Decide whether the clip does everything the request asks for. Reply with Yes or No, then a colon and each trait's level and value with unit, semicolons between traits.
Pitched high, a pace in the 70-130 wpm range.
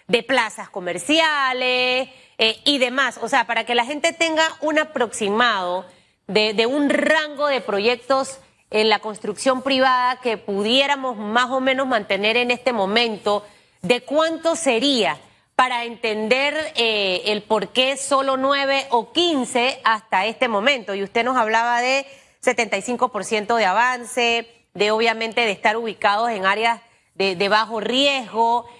No: high, 240 Hz; average, 145 wpm